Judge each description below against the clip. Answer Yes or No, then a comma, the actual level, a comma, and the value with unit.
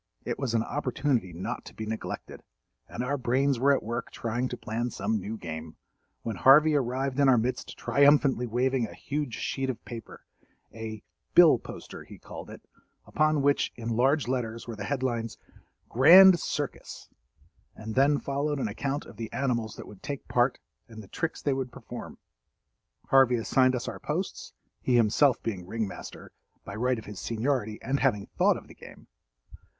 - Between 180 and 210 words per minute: No, average, 170 wpm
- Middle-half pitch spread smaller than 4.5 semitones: Yes, average, 3.6 semitones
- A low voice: Yes, low, 125 Hz